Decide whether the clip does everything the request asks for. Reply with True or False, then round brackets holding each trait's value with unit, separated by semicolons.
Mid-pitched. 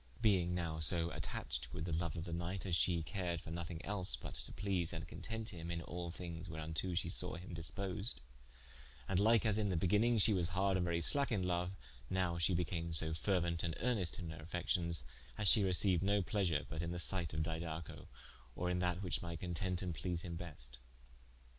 False (85 Hz)